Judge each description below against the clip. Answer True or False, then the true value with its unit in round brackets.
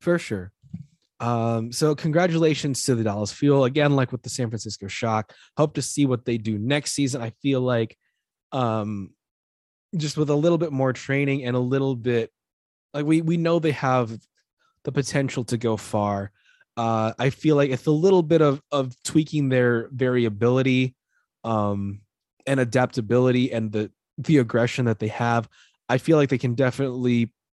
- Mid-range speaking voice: False (130 Hz)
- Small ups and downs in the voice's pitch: False (3.9 semitones)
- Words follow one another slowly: False (170 wpm)